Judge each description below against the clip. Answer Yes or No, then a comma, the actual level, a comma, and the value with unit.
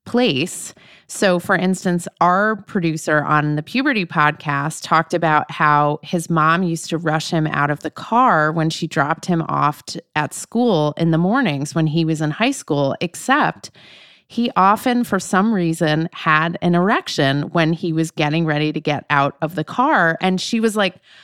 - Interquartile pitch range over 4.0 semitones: No, average, 3.4 semitones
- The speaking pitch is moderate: Yes, medium, 165 Hz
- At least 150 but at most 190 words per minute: Yes, average, 180 wpm